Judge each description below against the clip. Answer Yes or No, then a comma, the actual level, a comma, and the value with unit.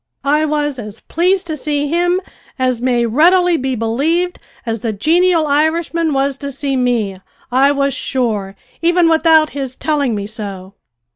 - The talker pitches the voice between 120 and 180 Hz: No, very high, 280 Hz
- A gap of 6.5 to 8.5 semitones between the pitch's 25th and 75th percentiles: No, average, 5.1 semitones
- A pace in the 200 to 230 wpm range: No, average, 155 wpm